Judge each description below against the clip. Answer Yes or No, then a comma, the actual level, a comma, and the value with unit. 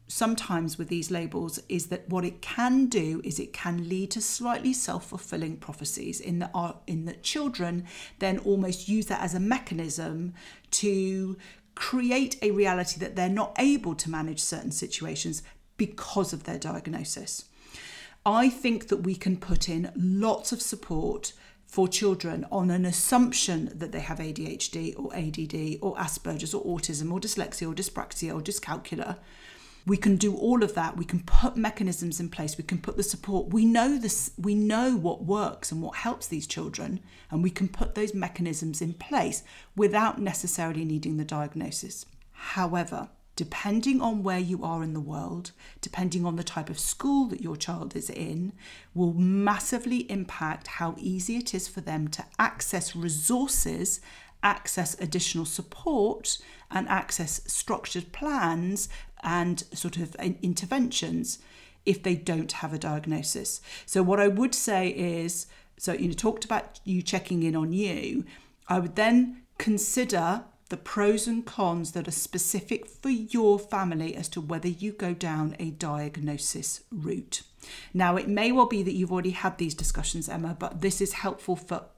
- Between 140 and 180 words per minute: Yes, average, 165 wpm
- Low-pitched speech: No, medium, 185 Hz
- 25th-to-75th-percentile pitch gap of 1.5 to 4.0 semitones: Yes, average, 3.6 semitones